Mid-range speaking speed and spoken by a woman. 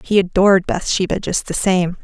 Yes: average, 175 wpm; female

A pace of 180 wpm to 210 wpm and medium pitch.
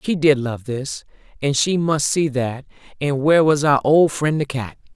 Yes: fast, 205 wpm; medium, 145 Hz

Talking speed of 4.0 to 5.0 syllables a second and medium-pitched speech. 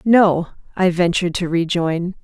Yes: 4.4 syllables/s; medium, 175 Hz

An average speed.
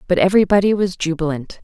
Yes: average, 145 wpm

